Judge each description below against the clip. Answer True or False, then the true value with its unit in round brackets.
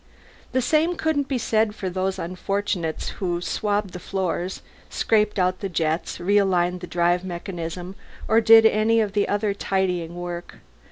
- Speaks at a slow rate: False (145 wpm)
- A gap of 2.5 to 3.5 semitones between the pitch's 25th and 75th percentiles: True (3.2 semitones)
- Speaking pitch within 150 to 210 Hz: True (190 Hz)